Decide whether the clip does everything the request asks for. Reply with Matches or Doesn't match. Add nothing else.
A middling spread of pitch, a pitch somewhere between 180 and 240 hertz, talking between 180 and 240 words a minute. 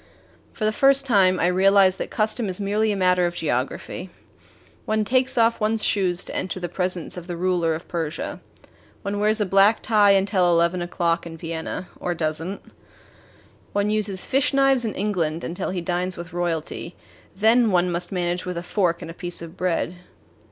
Matches